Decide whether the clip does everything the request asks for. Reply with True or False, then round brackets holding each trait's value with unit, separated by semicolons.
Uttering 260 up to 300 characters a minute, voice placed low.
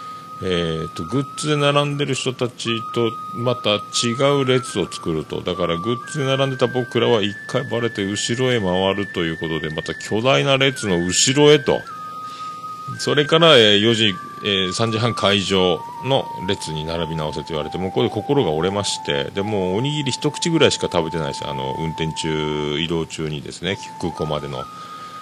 False (325 characters per minute; 115 Hz)